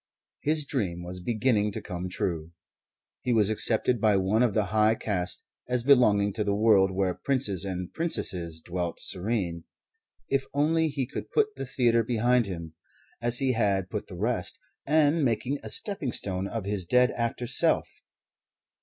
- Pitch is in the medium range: No, low, 110 Hz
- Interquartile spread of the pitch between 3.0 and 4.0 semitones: No, average, 4.9 semitones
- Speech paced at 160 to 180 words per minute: Yes, average, 165 wpm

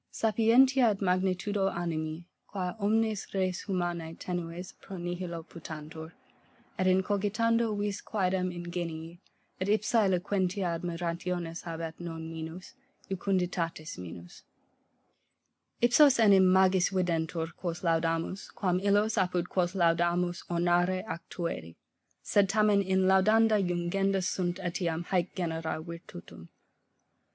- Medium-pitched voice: Yes, medium, 180 Hz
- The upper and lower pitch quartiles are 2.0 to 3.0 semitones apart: Yes, narrow, 2.6 semitones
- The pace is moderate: No, slow, 115 wpm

